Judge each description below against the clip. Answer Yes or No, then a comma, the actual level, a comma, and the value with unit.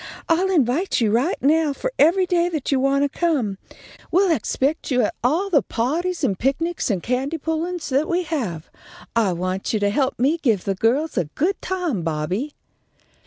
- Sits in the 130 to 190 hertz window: No, very high, 280 Hz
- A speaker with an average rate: Yes, average, 185 wpm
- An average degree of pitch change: No, wide, 6.7 semitones